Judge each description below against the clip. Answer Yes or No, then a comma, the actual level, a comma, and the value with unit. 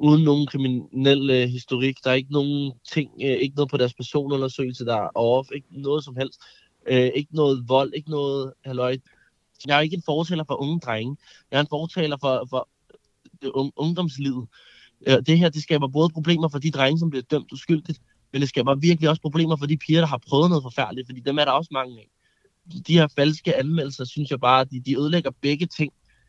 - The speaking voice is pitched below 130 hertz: No, medium, 140 Hz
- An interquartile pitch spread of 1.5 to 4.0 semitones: Yes, average, 2.8 semitones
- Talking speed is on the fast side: No, average, 205 wpm